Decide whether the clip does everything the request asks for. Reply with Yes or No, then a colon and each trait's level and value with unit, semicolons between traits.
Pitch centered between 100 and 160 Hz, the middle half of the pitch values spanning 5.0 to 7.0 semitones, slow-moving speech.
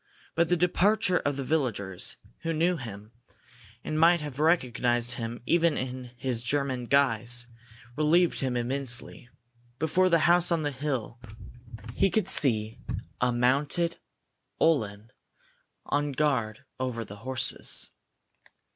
Yes: low, 135 Hz; average, 5.3 semitones; slow, 125 wpm